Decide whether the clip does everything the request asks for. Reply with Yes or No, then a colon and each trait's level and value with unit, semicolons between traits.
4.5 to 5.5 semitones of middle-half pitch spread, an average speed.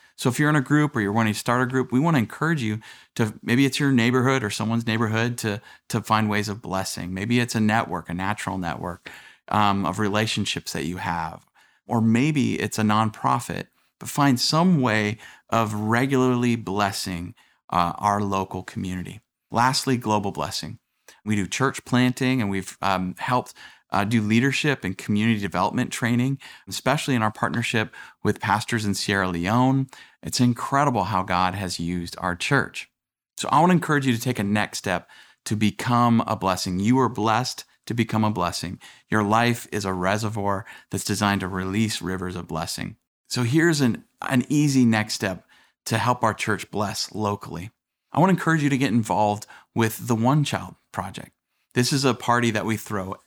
No: average, 4.1 semitones; average, 185 wpm